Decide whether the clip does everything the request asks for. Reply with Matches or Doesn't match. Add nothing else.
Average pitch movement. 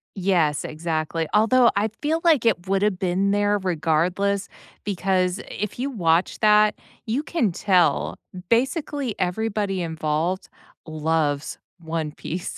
Matches